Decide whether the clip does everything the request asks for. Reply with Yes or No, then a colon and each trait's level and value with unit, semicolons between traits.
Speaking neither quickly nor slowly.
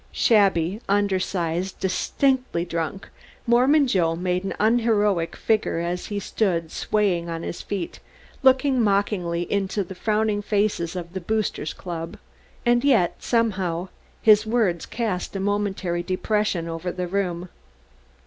No: slow, 130 wpm